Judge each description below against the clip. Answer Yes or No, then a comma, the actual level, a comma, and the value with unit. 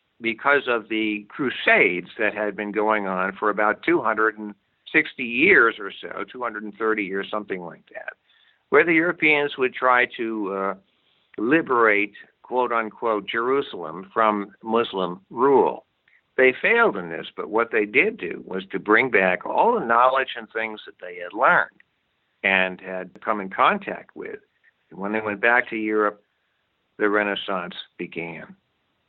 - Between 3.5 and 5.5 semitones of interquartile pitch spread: No, average, 2.8 semitones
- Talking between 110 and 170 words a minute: Yes, average, 150 wpm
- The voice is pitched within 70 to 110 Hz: Yes, low, 105 Hz